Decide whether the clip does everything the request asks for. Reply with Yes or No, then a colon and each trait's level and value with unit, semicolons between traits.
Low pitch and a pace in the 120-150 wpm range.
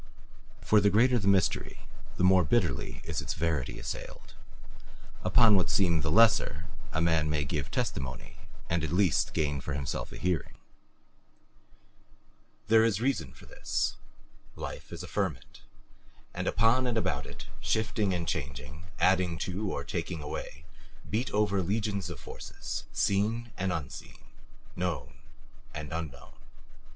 Yes: very low, 90 Hz; average, 140 wpm